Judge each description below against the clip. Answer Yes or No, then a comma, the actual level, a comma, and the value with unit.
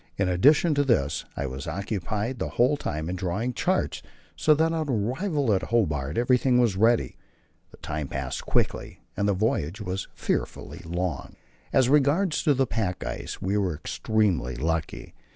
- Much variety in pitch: Yes, wide, 7.0 semitones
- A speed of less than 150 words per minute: No, average, 160 wpm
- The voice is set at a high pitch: No, low, 105 Hz